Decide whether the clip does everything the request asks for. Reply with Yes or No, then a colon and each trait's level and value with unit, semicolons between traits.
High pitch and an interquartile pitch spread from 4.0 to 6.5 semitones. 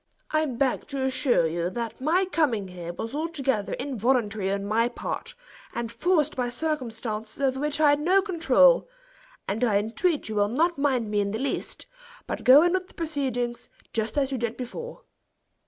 Yes: very high, 260 Hz; wide, 5.6 semitones